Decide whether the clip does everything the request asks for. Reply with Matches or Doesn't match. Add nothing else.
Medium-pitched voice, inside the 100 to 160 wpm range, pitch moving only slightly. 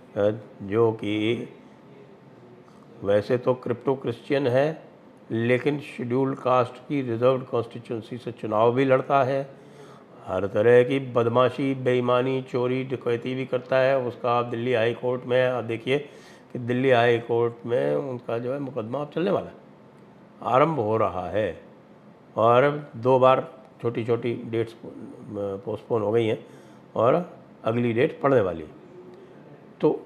Doesn't match